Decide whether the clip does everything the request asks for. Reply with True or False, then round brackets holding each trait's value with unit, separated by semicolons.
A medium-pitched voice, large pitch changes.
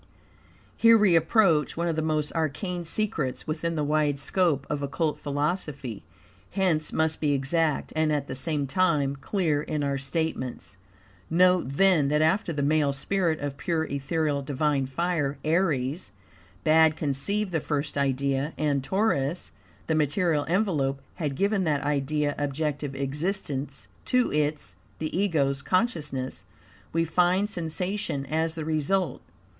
False (155 Hz; 3.4 semitones)